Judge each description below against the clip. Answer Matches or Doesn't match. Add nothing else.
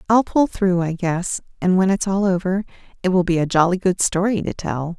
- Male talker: Doesn't match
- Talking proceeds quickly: Matches